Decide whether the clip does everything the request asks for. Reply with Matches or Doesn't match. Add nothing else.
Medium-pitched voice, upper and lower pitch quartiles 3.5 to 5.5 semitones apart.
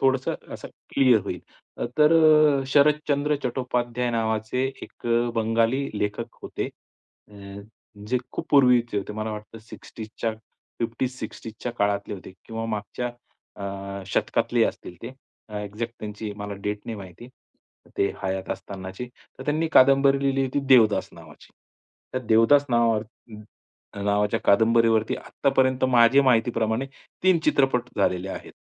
Doesn't match